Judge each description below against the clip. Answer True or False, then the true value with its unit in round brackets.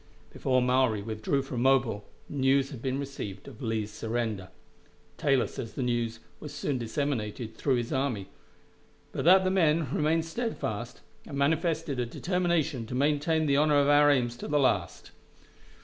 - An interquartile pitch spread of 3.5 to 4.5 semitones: True (3.9 semitones)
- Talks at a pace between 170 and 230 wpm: False (160 wpm)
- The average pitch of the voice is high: False (135 Hz)